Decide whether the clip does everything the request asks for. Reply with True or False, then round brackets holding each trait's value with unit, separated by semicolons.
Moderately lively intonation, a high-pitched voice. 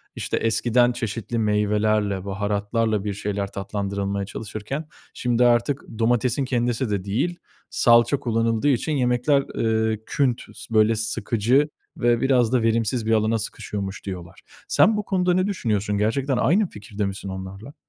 False (3.1 semitones; 115 Hz)